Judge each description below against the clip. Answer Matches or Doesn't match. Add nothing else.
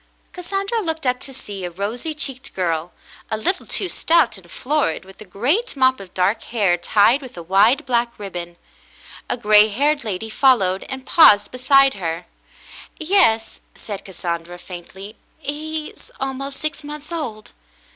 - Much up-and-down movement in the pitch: Matches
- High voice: Matches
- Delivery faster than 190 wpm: Doesn't match